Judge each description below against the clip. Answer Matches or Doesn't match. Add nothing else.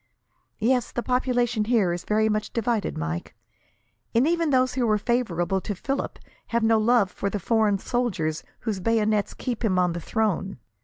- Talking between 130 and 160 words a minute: Doesn't match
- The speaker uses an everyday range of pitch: Matches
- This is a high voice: Matches